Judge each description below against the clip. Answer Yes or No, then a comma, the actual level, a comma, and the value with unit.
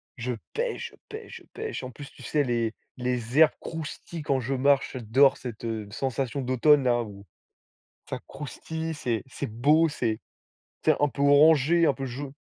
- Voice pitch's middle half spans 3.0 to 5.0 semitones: Yes, average, 3.8 semitones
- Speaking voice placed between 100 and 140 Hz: Yes, low, 135 Hz